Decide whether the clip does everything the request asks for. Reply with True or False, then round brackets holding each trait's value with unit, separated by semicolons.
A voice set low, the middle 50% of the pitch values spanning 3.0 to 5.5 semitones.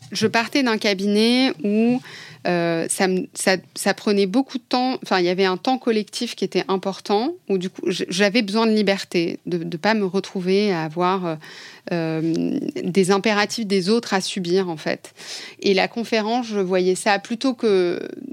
False (200 Hz; 3.5 semitones)